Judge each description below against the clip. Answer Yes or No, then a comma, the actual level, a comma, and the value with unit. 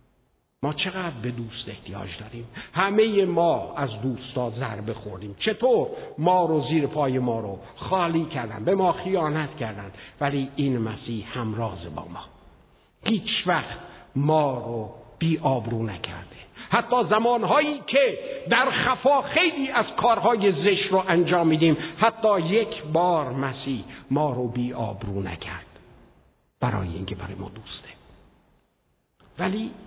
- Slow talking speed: No, average, 125 wpm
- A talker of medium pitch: Yes, medium, 145 Hz